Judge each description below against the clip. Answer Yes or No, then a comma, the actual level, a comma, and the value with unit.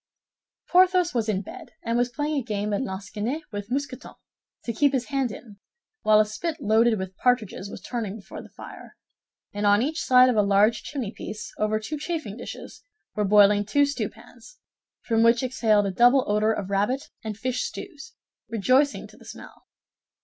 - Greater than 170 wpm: Yes, average, 180 wpm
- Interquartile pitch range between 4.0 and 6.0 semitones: Yes, average, 4.7 semitones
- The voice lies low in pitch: No, high, 230 Hz